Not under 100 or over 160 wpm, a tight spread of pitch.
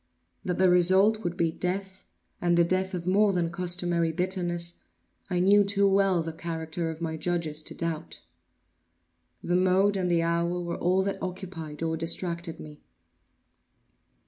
Yes: average, 155 wpm; narrow, 2.0 semitones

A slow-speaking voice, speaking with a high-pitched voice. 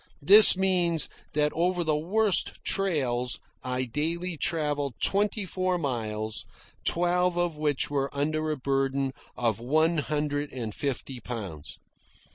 No: slow, 125 wpm; medium, 150 Hz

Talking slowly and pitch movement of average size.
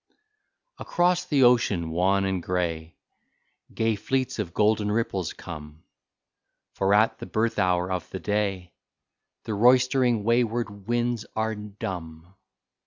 Yes: slow, 120 wpm; average, 4.3 semitones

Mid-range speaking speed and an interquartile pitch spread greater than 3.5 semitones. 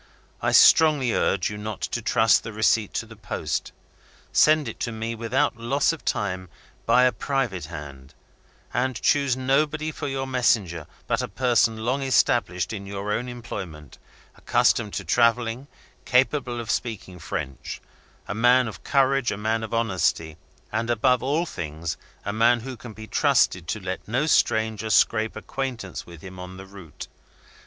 Yes: average, 165 wpm; average, 4.5 semitones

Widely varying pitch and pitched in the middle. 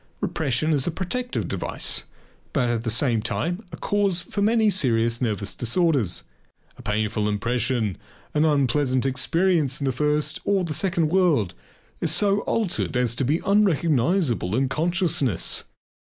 Yes: wide, 6.7 semitones; medium, 145 Hz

